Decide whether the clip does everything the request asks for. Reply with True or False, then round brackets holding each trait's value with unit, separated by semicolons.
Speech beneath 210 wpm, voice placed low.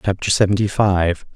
True (135 wpm; 95 Hz)